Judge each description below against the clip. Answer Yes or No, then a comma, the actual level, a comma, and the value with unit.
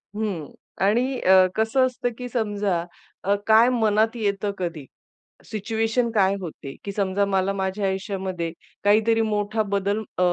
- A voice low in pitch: No, high, 205 Hz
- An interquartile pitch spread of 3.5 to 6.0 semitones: No, average, 2.7 semitones